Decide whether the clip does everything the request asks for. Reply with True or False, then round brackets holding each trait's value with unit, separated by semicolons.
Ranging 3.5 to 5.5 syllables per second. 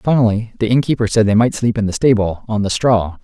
False (5.9 syllables/s)